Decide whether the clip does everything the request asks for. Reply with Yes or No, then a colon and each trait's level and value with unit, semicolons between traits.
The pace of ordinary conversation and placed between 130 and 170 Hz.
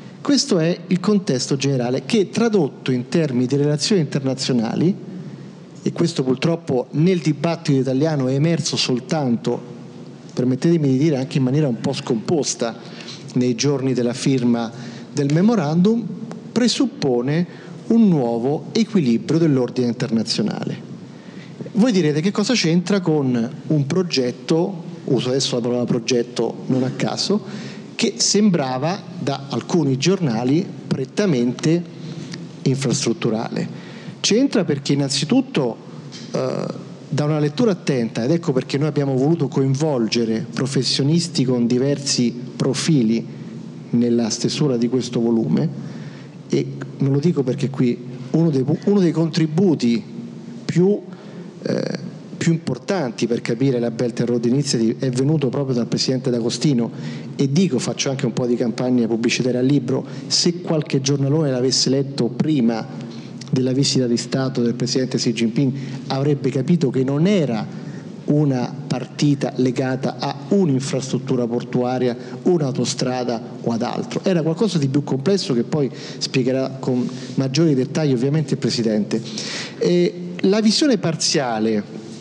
Yes: average, 125 wpm; medium, 140 Hz